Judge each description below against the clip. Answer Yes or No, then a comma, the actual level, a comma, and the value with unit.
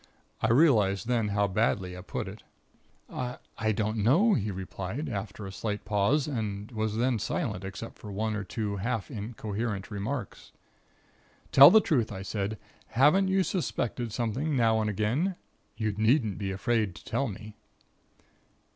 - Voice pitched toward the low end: Yes, low, 110 Hz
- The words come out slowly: No, average, 155 wpm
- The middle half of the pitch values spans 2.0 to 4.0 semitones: Yes, average, 3.4 semitones